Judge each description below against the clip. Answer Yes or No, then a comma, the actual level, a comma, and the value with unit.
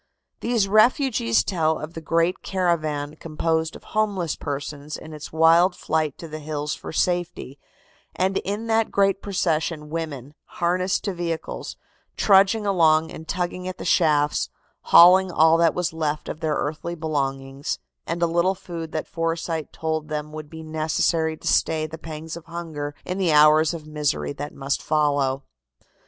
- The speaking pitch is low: No, medium, 160 Hz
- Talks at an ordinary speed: Yes, average, 160 wpm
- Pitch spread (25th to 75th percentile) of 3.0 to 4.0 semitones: No, narrow, 2.5 semitones